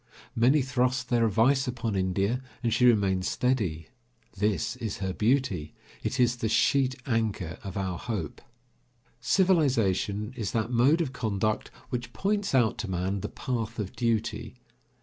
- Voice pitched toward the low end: Yes, low, 115 Hz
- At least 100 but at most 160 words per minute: Yes, average, 150 wpm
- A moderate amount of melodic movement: Yes, average, 4.1 semitones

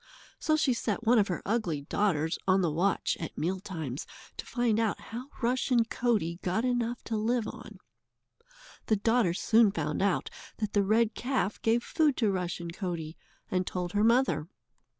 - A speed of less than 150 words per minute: No, average, 170 wpm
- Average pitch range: Yes, average, 4.9 semitones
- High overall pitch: Yes, high, 210 Hz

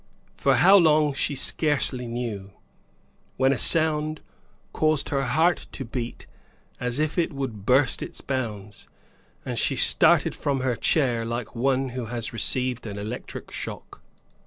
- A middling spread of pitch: Yes, average, 4.0 semitones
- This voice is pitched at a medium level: No, low, 130 Hz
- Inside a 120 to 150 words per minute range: Yes, average, 145 wpm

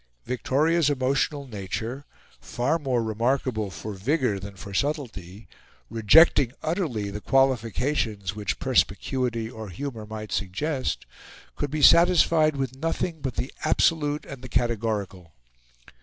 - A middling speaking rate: No, slow, 120 wpm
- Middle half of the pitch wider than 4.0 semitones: Yes, average, 5.2 semitones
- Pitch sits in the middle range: No, low, 125 Hz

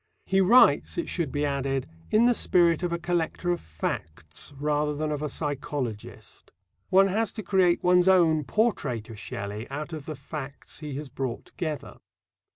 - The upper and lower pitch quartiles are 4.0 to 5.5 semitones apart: Yes, average, 4.6 semitones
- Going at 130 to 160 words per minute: No, average, 170 wpm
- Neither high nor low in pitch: Yes, medium, 150 Hz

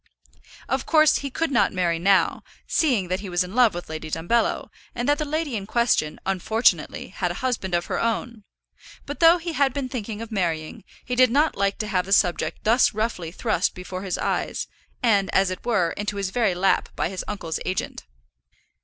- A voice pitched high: Yes, high, 210 Hz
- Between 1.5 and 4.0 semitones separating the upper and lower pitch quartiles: No, average, 5.3 semitones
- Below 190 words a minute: No, average, 200 wpm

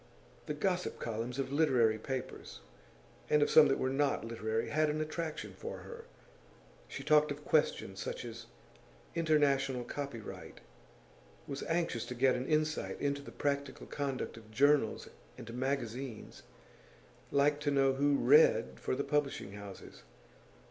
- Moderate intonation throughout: Yes, average, 3.5 semitones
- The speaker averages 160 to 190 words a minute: No, average, 140 wpm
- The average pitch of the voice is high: No, medium, 140 Hz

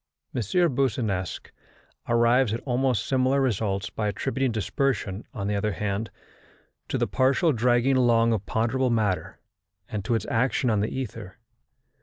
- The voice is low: Yes, low, 115 Hz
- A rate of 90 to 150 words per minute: Yes, average, 145 wpm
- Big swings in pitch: No, average, 3.7 semitones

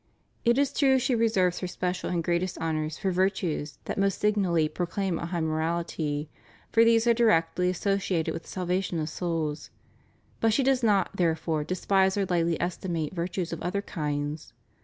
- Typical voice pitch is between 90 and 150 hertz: No, medium, 180 Hz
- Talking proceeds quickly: No, average, 175 wpm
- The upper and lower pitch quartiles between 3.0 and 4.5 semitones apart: Yes, average, 3.4 semitones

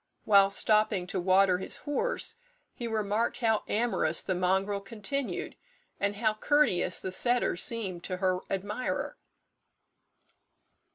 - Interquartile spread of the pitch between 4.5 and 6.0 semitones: No, average, 3.6 semitones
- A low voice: No, high, 205 Hz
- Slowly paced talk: Yes, slow, 120 wpm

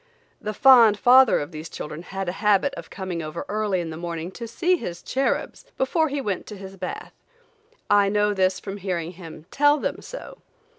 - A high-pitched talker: Yes, high, 200 Hz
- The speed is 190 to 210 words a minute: Yes, average, 195 wpm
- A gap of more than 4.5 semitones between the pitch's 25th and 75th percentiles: Yes, average, 5.3 semitones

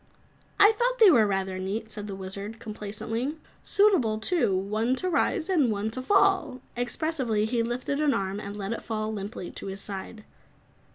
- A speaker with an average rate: Yes, average, 175 wpm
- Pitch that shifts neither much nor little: No, wide, 6.1 semitones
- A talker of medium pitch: No, high, 225 Hz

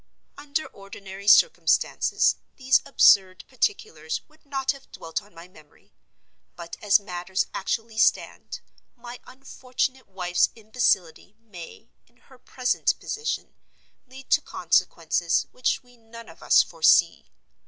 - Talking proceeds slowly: Yes, slow, 120 wpm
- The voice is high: Yes, high, 230 Hz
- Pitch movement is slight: No, wide, 5.5 semitones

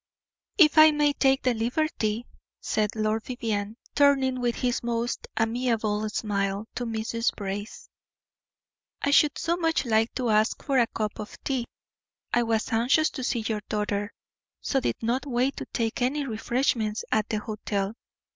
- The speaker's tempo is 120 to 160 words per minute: Yes, average, 155 wpm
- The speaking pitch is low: No, high, 230 Hz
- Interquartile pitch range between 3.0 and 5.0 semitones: Yes, average, 3.4 semitones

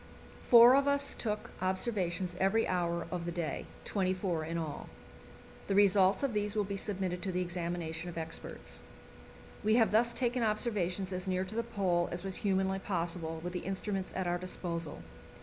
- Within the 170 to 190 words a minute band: Yes, average, 180 wpm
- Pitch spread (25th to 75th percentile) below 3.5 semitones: Yes, average, 3.1 semitones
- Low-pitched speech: No, medium, 185 Hz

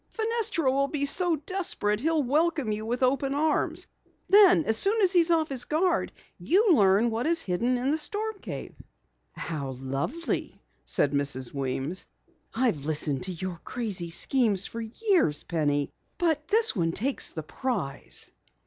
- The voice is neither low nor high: No, very high, 255 Hz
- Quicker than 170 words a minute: No, average, 155 wpm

